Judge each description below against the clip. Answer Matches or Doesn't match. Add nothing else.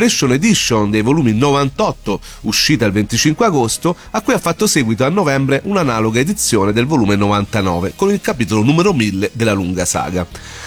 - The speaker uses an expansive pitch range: Matches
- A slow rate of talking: Doesn't match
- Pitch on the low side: Matches